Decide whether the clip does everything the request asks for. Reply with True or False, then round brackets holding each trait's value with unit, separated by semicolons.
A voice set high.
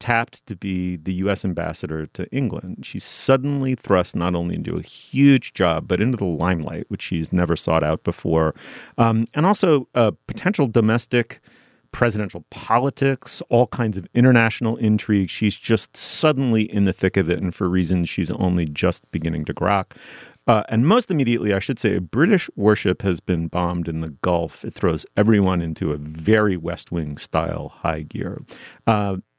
False (100 Hz)